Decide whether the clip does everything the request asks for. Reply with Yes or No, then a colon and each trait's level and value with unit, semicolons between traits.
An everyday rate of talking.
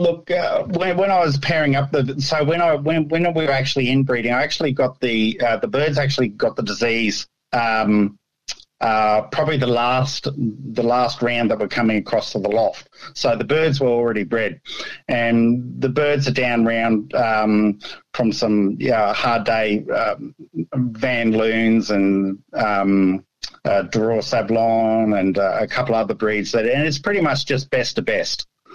Yes: average, 175 wpm